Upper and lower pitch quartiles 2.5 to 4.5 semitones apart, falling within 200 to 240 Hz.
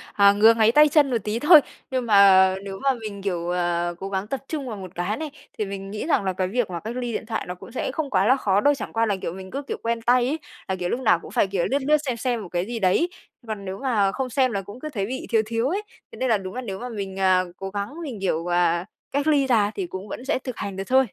No: average, 5.0 semitones; high, 215 Hz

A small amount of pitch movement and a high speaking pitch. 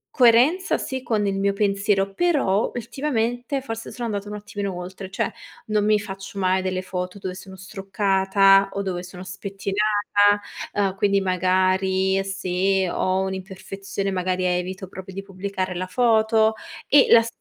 Yes: narrow, 2.0 semitones; high, 195 Hz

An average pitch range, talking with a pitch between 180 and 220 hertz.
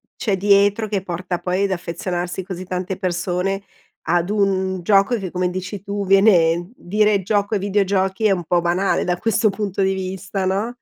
No: narrow, 2.0 semitones; high, 190 Hz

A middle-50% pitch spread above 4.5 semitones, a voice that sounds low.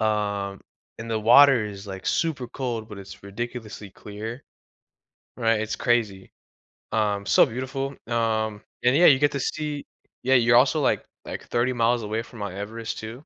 No: average, 3.2 semitones; low, 115 Hz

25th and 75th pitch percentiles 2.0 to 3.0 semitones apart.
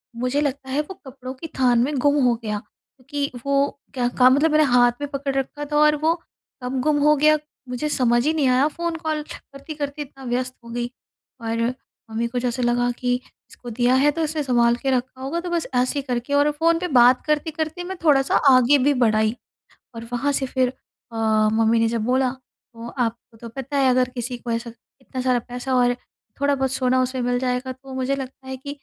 Yes: average, 2.7 semitones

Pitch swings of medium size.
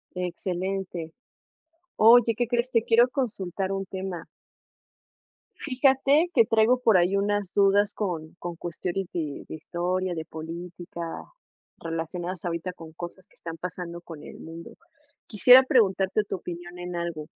Yes: average, 3.7 semitones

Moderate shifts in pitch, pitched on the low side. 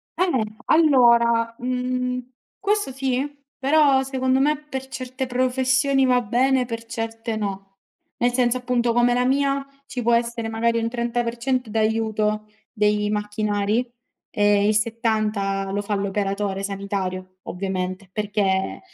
No: average, 3.6 semitones; high, 235 Hz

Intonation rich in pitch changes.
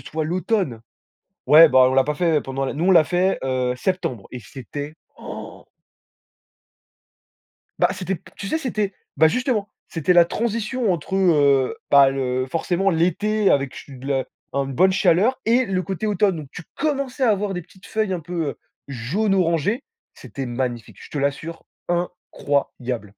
Yes: wide, 6.1 semitones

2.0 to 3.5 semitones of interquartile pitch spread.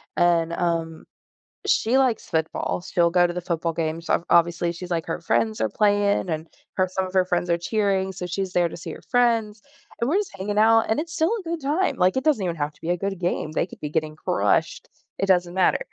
No: average, 4.1 semitones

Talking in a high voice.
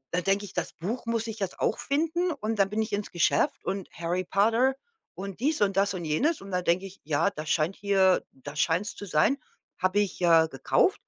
Yes: high, 195 Hz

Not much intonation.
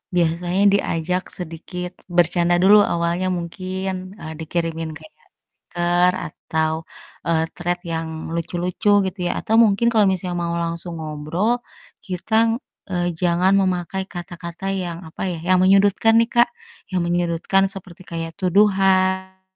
Yes: narrow, 2.0 semitones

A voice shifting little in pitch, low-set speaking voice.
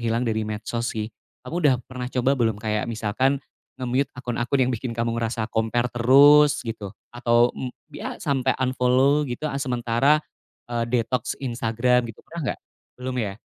Yes: narrow, 2.3 semitones; low, 120 Hz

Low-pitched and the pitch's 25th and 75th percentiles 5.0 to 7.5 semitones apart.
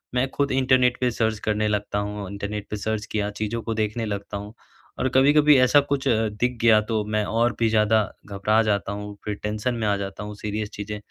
No: low, 110 Hz; narrow, 2.5 semitones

